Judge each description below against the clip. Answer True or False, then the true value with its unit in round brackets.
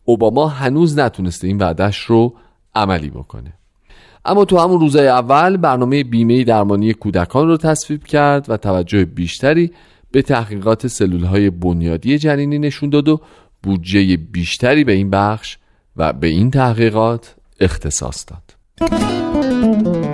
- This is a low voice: True (115 Hz)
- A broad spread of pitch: True (7.3 semitones)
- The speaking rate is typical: True (130 wpm)